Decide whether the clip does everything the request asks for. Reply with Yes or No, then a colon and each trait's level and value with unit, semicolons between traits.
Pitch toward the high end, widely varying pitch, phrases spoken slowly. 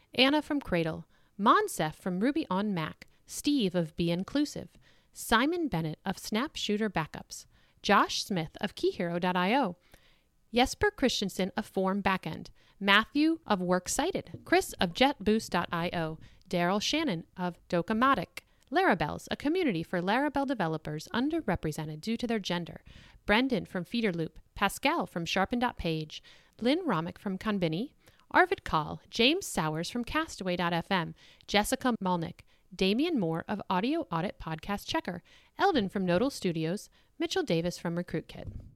Yes: high, 200 Hz; wide, 7.2 semitones; slow, 125 wpm